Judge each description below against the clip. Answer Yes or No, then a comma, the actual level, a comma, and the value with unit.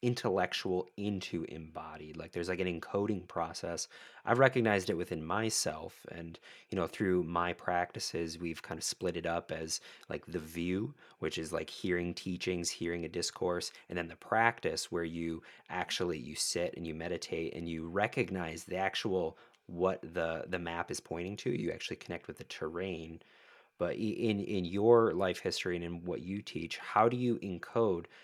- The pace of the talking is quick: No, average, 175 wpm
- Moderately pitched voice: No, very low, 90 Hz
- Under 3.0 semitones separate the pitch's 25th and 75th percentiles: No, average, 3.3 semitones